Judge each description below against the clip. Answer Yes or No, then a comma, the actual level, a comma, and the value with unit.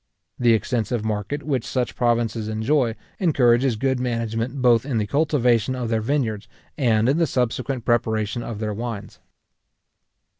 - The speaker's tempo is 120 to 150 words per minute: Yes, average, 145 wpm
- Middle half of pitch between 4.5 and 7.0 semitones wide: No, average, 2.8 semitones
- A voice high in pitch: No, low, 120 Hz